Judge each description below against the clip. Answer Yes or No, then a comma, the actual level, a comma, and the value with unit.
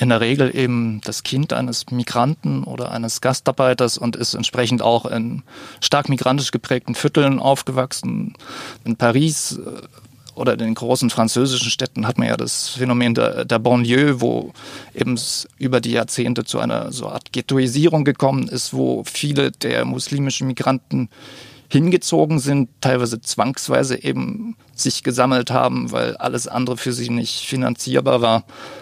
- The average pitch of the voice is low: Yes, low, 125 Hz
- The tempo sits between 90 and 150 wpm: Yes, average, 145 wpm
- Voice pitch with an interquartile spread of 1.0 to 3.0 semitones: Yes, narrow, 2.4 semitones